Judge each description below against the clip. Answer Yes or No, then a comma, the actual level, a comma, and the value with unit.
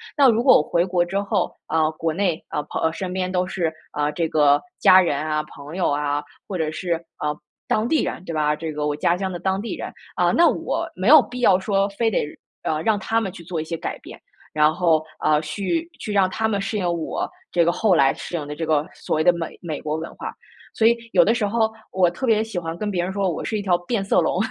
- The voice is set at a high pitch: No, medium, 175 Hz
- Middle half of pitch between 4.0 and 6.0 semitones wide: Yes, average, 4.3 semitones